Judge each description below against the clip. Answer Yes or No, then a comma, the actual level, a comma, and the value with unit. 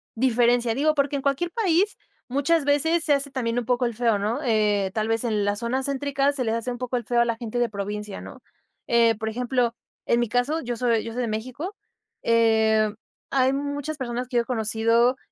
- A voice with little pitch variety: No, average, 3.4 semitones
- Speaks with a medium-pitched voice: No, high, 240 Hz